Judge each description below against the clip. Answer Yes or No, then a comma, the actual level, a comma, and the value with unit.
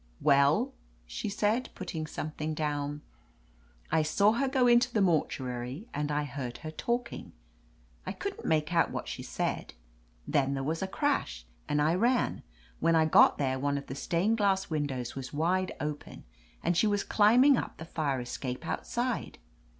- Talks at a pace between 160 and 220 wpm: Yes, average, 175 wpm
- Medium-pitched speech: Yes, medium, 155 Hz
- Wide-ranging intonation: Yes, wide, 6.5 semitones